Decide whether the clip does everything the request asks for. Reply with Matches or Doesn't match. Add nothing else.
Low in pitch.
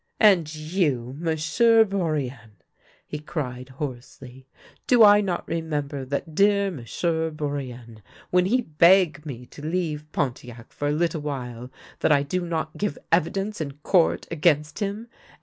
Doesn't match